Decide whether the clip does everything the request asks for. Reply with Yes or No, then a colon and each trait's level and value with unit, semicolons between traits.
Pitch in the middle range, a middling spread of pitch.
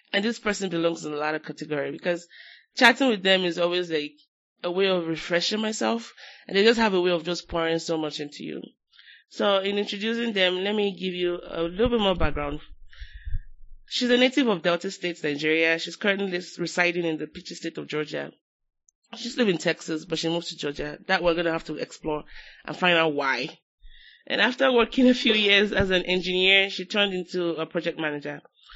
Yes: medium, 175 Hz; average, 3.8 semitones